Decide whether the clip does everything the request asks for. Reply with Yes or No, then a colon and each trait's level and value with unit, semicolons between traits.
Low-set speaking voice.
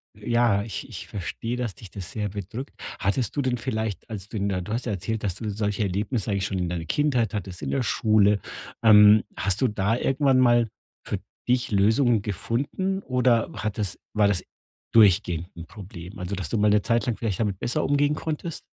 Yes: low, 105 Hz